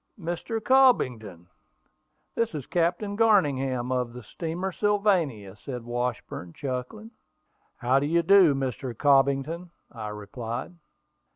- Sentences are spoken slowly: Yes, slow, 110 wpm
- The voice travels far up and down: Yes, wide, 6.8 semitones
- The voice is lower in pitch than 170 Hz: Yes, medium, 140 Hz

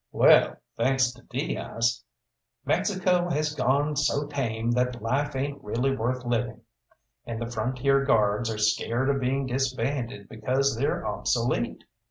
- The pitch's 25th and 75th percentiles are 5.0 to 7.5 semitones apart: No, average, 3.0 semitones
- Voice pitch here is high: No, low, 130 Hz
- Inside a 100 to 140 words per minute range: Yes, slow, 135 wpm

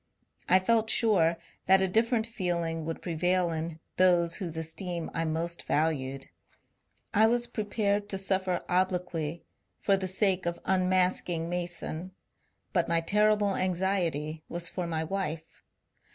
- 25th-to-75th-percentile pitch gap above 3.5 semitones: No, average, 2.7 semitones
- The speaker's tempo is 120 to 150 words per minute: Yes, average, 140 wpm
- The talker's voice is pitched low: No, medium, 180 Hz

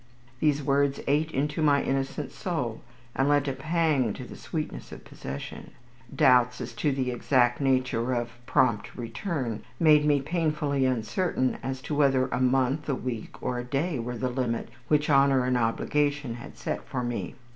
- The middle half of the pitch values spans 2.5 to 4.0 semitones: Yes, average, 2.9 semitones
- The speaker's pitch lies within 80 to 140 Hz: Yes, low, 135 Hz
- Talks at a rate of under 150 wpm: No, average, 170 wpm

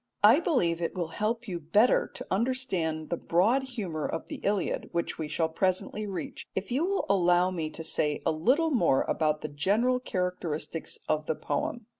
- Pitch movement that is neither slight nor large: No, wide, 6.1 semitones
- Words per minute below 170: No, average, 185 wpm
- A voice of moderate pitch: Yes, medium, 180 Hz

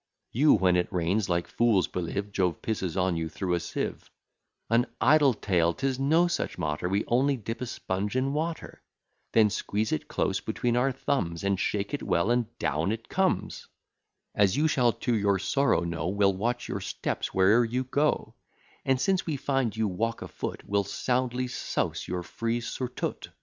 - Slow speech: No, average, 180 wpm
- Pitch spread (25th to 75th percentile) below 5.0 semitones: No, wide, 5.5 semitones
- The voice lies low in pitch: Yes, low, 110 Hz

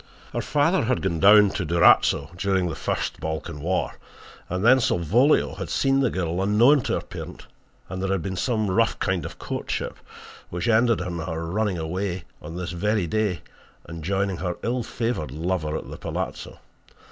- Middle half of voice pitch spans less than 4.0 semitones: No, average, 4.3 semitones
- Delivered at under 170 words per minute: No, average, 180 wpm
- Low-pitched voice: Yes, very low, 95 Hz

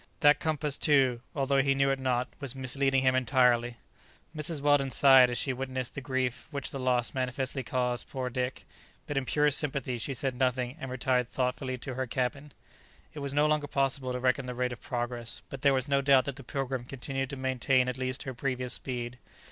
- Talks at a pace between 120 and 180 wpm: No, fast, 205 wpm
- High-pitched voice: No, low, 130 Hz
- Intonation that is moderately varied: No, narrow, 1.6 semitones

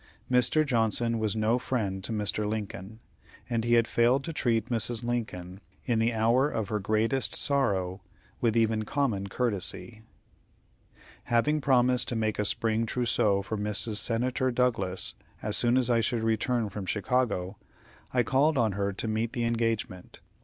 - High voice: No, low, 115 Hz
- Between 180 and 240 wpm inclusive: No, average, 160 wpm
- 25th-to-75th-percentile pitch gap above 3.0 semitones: No, narrow, 2.6 semitones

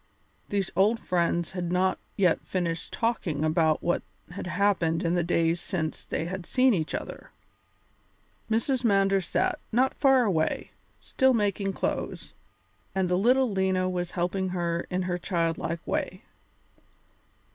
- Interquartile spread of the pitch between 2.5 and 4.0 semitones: Yes, average, 2.9 semitones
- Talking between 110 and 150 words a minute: Yes, average, 140 wpm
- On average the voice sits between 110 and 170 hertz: No, medium, 185 Hz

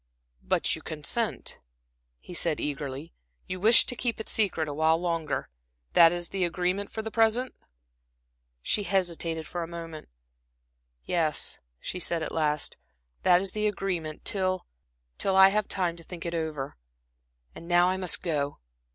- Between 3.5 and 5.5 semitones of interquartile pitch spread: No, average, 3.1 semitones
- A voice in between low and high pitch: Yes, medium, 175 Hz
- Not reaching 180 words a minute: Yes, average, 155 wpm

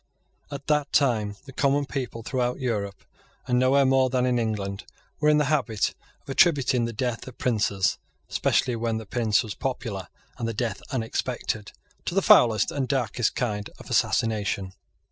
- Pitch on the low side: Yes, low, 120 Hz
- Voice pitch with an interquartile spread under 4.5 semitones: Yes, average, 3.5 semitones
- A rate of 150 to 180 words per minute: Yes, average, 165 wpm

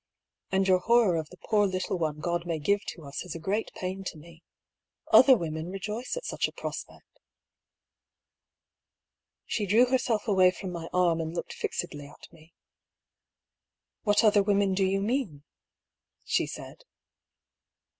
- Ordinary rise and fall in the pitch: Yes, average, 3.7 semitones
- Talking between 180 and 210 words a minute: No, average, 165 wpm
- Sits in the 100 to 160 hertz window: No, medium, 185 Hz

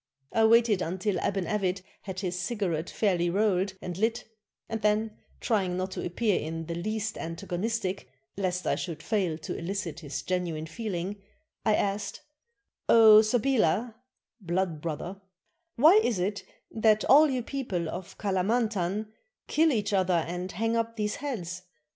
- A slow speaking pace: No, average, 150 wpm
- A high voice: Yes, high, 195 Hz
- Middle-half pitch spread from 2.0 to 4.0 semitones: Yes, average, 3.7 semitones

